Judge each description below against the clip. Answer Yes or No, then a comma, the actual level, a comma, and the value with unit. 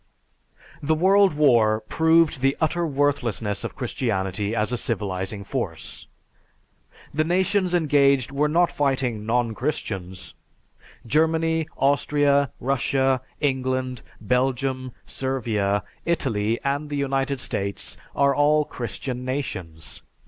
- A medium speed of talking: No, slow, 110 wpm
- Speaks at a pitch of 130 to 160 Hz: Yes, low, 135 Hz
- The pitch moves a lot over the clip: No, average, 4.5 semitones